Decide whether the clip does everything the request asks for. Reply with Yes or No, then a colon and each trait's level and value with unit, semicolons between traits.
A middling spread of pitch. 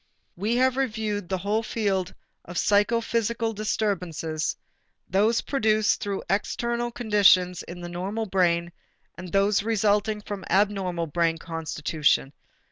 Yes: average, 3.8 semitones